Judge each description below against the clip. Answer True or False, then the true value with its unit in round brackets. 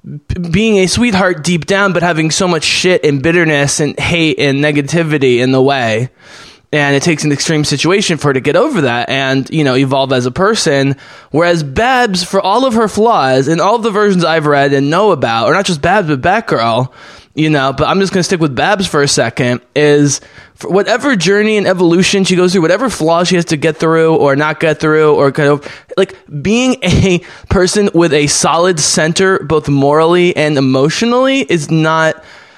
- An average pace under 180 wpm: False (205 wpm)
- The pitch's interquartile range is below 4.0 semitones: False (4.5 semitones)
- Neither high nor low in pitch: True (160 Hz)